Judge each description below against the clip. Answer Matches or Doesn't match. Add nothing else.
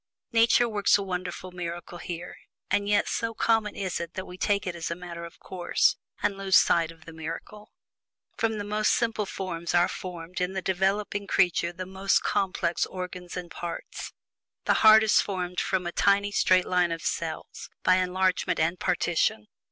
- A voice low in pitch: Doesn't match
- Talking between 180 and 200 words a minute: Matches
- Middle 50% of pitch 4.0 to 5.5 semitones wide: Doesn't match